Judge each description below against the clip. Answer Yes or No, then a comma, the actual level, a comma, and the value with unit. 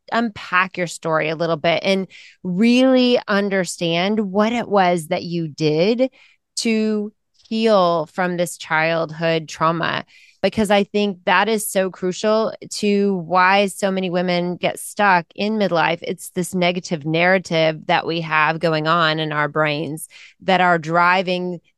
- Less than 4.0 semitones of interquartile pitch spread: Yes, average, 3.5 semitones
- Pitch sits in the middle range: Yes, medium, 180 Hz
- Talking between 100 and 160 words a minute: Yes, average, 145 wpm